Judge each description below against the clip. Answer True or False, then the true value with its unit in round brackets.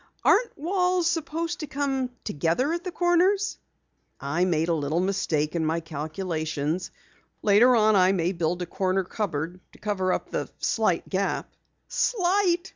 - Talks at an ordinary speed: True (150 wpm)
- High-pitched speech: True (195 Hz)